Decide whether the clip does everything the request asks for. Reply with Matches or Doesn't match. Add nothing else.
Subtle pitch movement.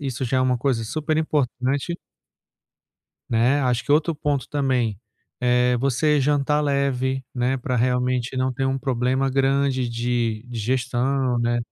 Matches